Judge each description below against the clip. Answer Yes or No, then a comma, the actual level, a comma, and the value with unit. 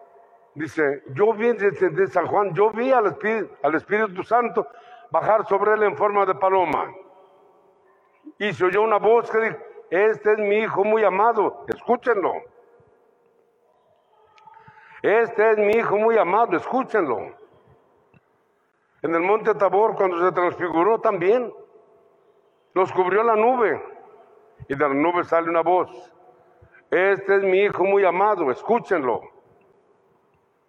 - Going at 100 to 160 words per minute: Yes, average, 130 wpm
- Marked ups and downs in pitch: No, average, 3.8 semitones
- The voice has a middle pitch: No, high, 210 Hz